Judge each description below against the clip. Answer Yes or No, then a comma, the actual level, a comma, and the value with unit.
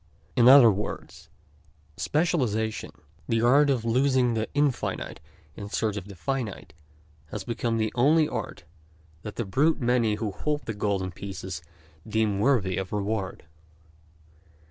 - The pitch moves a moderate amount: Yes, average, 4.2 semitones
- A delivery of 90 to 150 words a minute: Yes, slow, 135 wpm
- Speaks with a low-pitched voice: Yes, low, 115 Hz